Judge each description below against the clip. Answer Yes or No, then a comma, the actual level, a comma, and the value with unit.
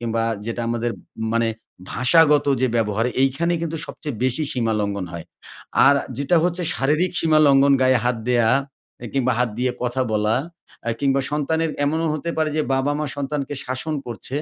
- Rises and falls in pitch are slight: No, average, 4.3 semitones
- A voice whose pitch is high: No, low, 135 Hz